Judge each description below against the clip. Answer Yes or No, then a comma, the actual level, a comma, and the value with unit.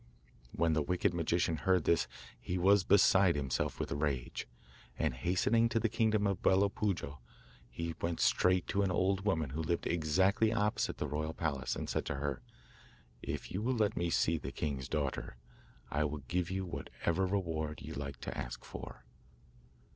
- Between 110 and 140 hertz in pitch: No, very low, 85 Hz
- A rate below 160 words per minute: No, average, 175 wpm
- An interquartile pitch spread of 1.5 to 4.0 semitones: No, average, 4.5 semitones